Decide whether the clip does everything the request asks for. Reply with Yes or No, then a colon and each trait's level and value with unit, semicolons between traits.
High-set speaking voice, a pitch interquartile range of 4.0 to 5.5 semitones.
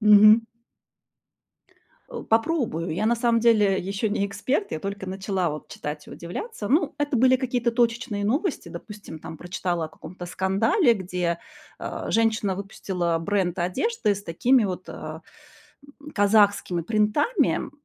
Yes: high, 205 Hz; average, 4.5 semitones